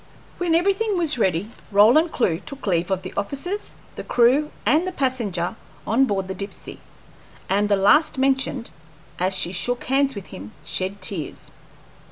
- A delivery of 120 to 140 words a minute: No, average, 160 wpm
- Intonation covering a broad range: Yes, wide, 6.9 semitones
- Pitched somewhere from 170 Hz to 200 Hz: No, high, 230 Hz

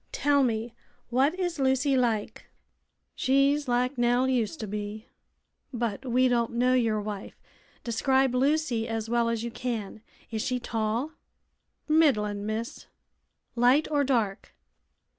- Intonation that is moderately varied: Yes, average, 3.1 semitones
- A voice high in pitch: Yes, high, 245 Hz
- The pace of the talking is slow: Yes, slow, 130 wpm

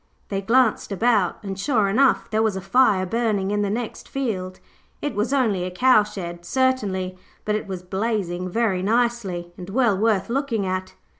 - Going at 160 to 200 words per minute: Yes, average, 170 wpm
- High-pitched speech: Yes, high, 205 Hz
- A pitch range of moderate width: Yes, average, 4.0 semitones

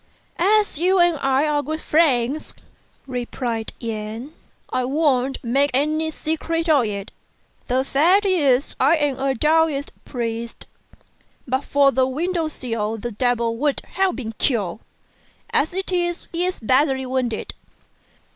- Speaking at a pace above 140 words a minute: No, slow, 135 wpm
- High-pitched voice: Yes, very high, 275 Hz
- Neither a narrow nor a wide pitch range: Yes, average, 4.6 semitones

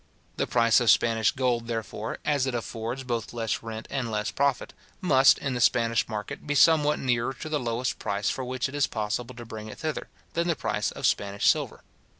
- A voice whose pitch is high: No, low, 120 Hz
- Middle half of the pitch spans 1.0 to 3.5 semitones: Yes, average, 3.1 semitones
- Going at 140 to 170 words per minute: No, fast, 205 wpm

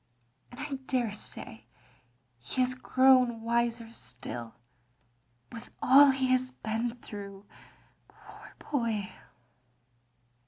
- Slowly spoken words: Yes, slow, 90 wpm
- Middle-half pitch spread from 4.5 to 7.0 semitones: No, average, 3.4 semitones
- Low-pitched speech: No, high, 235 Hz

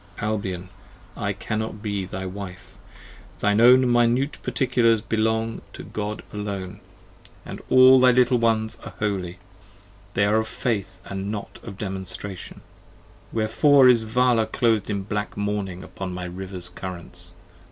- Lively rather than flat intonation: No, average, 3.2 semitones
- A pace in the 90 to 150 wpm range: Yes, average, 140 wpm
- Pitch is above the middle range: No, low, 105 Hz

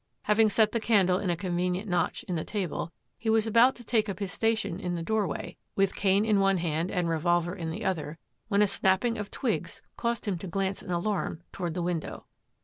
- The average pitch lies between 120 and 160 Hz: No, high, 190 Hz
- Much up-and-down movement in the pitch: No, average, 3.5 semitones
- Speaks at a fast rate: Yes, fast, 220 wpm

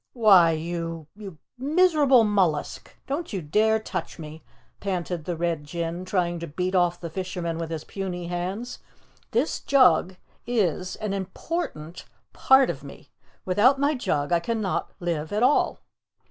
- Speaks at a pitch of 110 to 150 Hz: No, medium, 185 Hz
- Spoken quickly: No, average, 145 wpm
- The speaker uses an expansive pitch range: No, average, 4.7 semitones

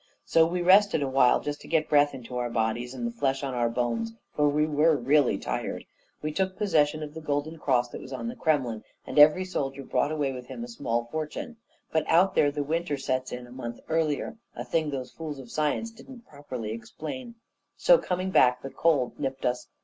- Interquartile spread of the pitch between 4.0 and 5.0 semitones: Yes, average, 4.3 semitones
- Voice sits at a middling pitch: Yes, medium, 145 Hz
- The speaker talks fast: Yes, fast, 215 wpm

